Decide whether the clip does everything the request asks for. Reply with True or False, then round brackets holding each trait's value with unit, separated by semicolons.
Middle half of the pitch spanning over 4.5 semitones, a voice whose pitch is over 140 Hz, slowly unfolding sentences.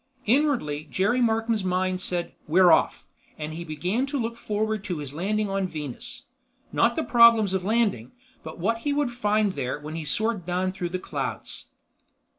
False (5.2 semitones; 190 Hz; 175 wpm)